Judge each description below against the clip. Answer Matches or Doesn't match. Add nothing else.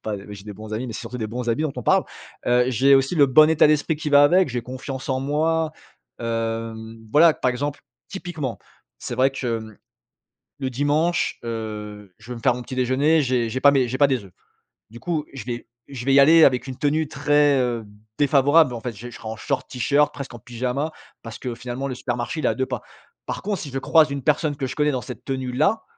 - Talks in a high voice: Doesn't match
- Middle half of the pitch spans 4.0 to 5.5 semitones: Doesn't match